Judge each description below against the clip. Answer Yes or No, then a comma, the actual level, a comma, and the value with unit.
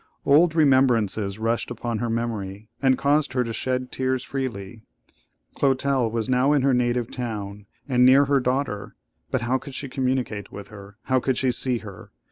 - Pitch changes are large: No, average, 3.1 semitones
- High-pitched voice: No, low, 125 Hz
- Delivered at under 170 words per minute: No, average, 175 wpm